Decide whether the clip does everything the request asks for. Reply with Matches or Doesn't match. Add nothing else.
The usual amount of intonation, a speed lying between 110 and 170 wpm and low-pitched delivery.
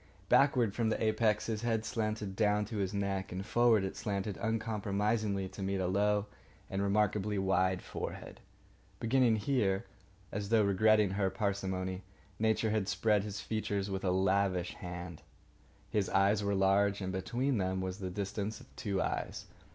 Doesn't match